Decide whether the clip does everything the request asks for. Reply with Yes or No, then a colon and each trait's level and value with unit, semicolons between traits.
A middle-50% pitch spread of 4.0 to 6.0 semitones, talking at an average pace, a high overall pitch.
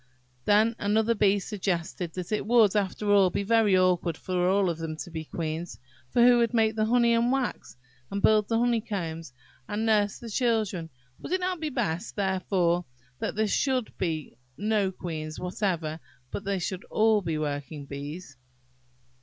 Yes: average, 4.5 semitones; average, 170 wpm; high, 200 Hz